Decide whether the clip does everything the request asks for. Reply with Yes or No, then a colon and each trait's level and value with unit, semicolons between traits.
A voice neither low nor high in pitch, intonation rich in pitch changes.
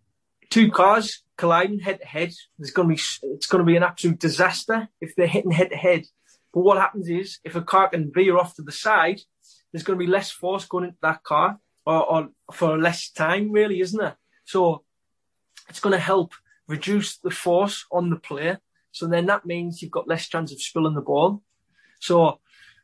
No: medium, 175 Hz; average, 2.8 semitones